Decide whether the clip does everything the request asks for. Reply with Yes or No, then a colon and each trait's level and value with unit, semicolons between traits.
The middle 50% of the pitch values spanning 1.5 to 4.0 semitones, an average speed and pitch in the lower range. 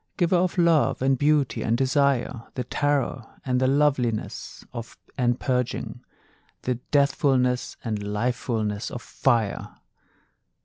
No: average, 3.1 semitones; slow, 115 wpm; low, 130 Hz